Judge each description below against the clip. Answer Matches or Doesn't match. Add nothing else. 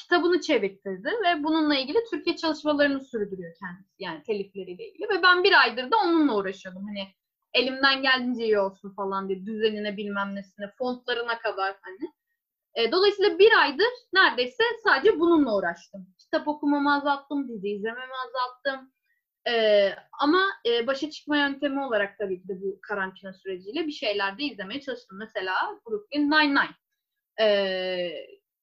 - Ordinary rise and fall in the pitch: Doesn't match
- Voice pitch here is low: Doesn't match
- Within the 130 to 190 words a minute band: Matches